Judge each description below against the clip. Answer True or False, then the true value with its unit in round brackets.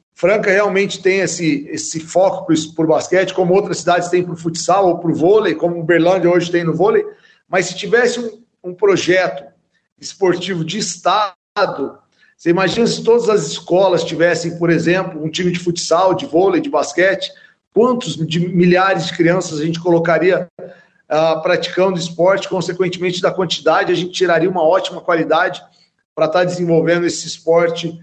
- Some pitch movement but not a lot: False (2.1 semitones)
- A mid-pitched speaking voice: True (180 Hz)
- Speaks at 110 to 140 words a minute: False (170 wpm)